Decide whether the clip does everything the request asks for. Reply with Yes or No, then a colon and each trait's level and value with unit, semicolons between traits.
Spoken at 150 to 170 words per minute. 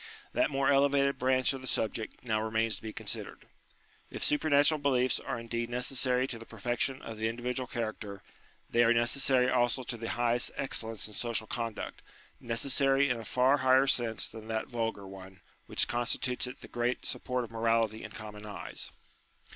No: average, 180 wpm